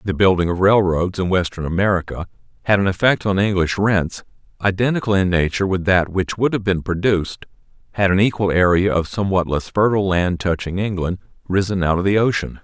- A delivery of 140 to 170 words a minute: No, average, 185 wpm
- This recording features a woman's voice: No, male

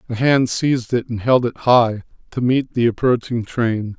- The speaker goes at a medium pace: Yes, average, 195 wpm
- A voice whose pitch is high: No, low, 120 Hz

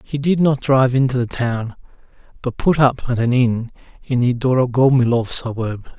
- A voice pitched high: No, low, 125 Hz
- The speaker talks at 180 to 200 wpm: No, average, 170 wpm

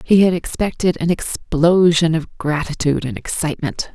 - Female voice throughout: Yes, female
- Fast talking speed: No, slow, 135 wpm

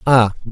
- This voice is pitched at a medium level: No, low, 120 Hz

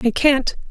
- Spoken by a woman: Yes, female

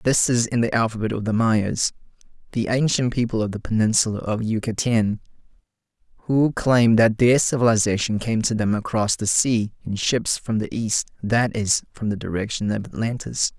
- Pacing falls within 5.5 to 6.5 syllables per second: No, 5.0 syllables/s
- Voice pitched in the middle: No, low, 110 Hz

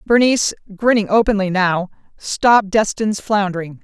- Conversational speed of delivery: No, slow, 110 wpm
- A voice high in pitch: Yes, high, 205 Hz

